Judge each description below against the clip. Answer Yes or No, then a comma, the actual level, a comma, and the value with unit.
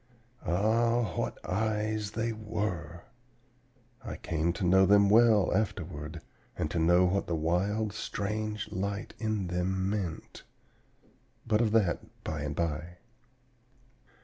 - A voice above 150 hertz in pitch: No, low, 100 Hz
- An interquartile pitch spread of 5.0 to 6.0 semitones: No, average, 3.8 semitones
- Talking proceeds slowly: Yes, slow, 120 wpm